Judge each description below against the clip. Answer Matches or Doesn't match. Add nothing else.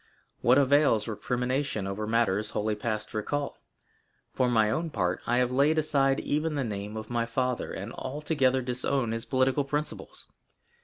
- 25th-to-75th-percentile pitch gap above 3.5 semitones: Matches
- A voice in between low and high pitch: Doesn't match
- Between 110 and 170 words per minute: Matches